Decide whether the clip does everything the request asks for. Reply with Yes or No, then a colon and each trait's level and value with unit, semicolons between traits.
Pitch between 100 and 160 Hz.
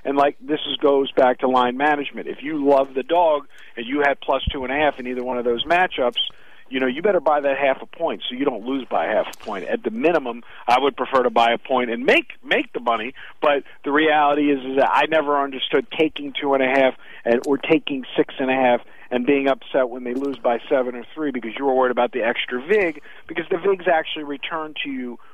Yes: medium, 140 Hz